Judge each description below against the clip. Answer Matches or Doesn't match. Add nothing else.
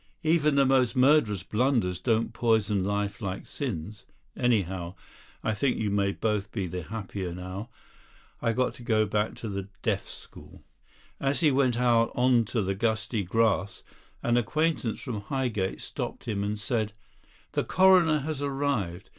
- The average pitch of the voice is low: Matches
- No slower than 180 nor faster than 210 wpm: Doesn't match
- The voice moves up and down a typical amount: Matches